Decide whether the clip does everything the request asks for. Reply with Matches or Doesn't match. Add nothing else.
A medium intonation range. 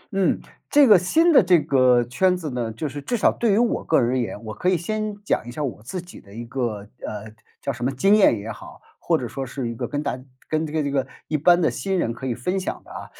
Doesn't match